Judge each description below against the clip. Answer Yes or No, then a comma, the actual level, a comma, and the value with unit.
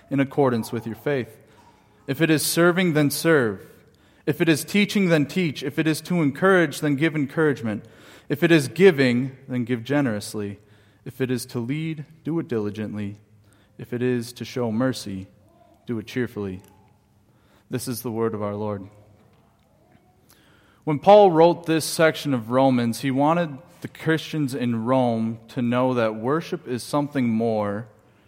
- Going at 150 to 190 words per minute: Yes, average, 160 wpm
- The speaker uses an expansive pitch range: Yes, wide, 5.9 semitones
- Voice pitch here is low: Yes, low, 125 Hz